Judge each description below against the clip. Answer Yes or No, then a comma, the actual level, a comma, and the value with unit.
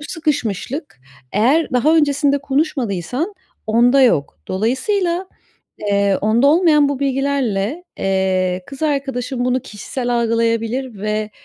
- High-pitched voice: Yes, very high, 255 Hz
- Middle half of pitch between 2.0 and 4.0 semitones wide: No, average, 5.0 semitones